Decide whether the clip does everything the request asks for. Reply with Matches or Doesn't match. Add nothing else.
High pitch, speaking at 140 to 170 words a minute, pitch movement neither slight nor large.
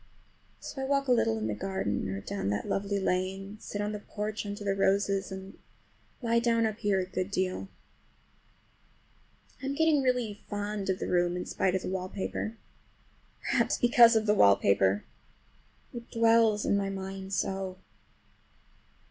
Matches